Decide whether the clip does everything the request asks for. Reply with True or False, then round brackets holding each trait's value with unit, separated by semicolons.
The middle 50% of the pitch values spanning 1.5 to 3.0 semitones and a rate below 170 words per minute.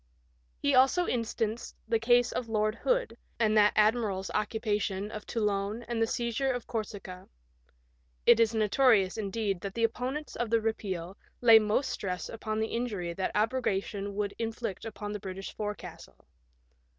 True (2.4 semitones; 150 wpm)